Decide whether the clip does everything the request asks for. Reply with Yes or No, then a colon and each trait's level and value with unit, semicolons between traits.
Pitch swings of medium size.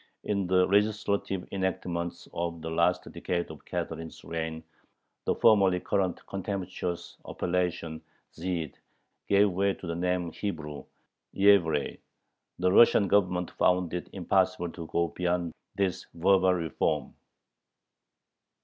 No: narrow, 2.3 semitones